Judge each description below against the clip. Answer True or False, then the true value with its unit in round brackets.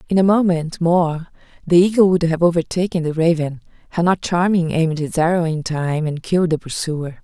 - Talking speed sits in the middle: True (190 wpm)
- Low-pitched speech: False (170 Hz)